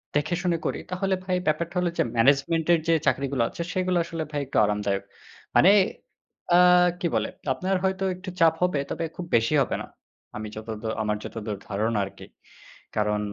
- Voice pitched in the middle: Yes, medium, 155 Hz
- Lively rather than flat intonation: Yes, wide, 8.4 semitones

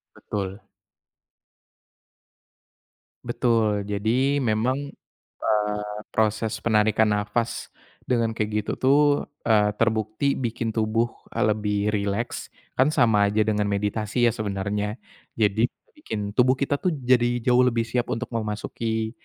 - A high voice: No, low, 110 Hz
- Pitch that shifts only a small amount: Yes, narrow, 2.0 semitones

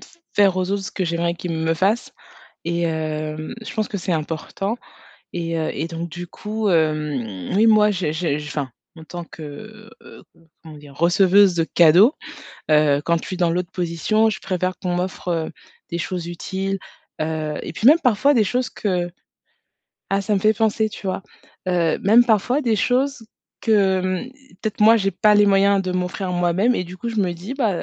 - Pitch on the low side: No, medium, 185 Hz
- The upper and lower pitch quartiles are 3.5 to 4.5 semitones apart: Yes, average, 4.1 semitones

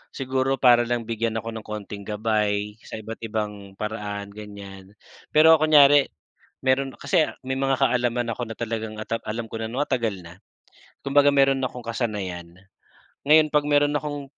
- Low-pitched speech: Yes, low, 115 Hz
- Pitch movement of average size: Yes, average, 4.3 semitones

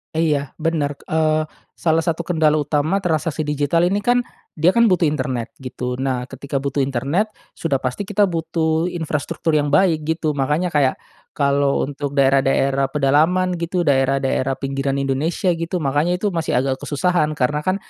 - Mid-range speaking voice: Yes, medium, 150 Hz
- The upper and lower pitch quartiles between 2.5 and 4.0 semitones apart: Yes, average, 3.5 semitones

